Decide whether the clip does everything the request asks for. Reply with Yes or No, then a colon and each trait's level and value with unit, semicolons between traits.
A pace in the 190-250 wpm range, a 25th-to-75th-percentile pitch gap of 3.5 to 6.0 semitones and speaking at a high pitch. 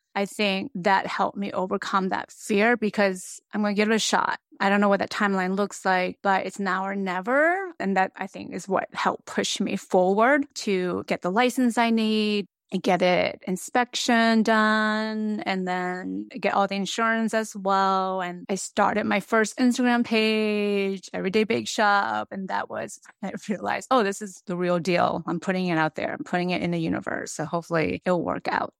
No: average, 200 wpm; average, 2.8 semitones; high, 200 Hz